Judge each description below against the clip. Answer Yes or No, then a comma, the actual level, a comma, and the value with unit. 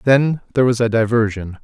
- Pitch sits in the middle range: No, low, 115 Hz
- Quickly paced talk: No, average, 185 wpm